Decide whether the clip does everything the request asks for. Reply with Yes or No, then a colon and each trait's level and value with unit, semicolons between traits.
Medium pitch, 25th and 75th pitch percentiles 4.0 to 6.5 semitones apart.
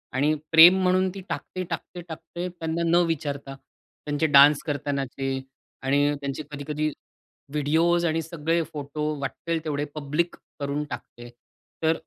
No: medium, 155 Hz; average, 2.8 semitones